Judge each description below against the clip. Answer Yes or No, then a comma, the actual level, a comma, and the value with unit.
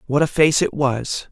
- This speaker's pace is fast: Yes, fast, 230 wpm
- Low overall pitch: No, medium, 145 Hz